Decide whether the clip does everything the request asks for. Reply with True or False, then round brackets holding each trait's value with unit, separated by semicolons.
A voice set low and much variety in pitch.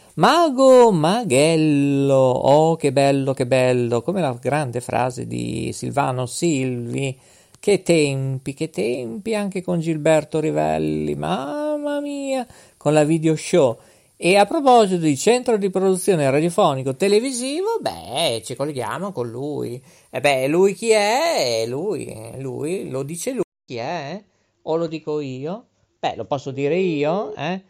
False (155 Hz; 7.0 semitones)